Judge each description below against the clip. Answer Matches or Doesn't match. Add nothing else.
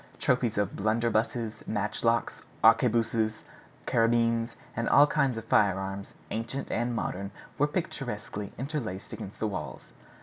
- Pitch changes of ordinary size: Doesn't match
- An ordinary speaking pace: Doesn't match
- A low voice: Matches